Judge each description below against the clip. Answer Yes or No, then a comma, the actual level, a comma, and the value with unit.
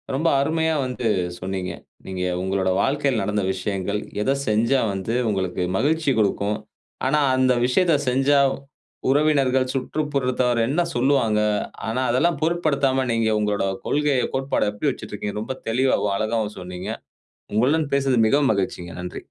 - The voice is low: Yes, low, 125 Hz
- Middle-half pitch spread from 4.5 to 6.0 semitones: Yes, average, 5.2 semitones